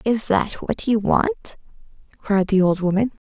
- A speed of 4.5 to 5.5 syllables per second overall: No, 4.1 syllables/s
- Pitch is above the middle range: Yes, high, 200 Hz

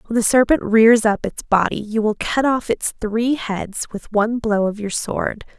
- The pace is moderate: No, fast, 215 wpm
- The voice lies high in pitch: Yes, high, 220 Hz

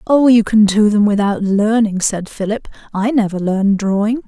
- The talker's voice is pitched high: Yes, high, 210 Hz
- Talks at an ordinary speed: Yes, average, 180 wpm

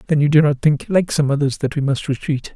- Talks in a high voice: No, medium, 150 Hz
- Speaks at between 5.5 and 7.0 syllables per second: Yes, 6.0 syllables/s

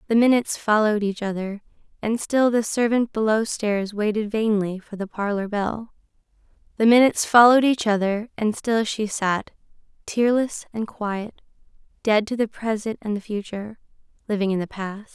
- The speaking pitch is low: No, high, 215 Hz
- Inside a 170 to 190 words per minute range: No, average, 160 wpm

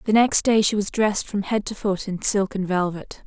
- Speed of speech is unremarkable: No, fast, 255 wpm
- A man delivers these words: No, female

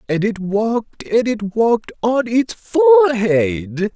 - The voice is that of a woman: No, male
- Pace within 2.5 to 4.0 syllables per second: Yes, 3.5 syllables/s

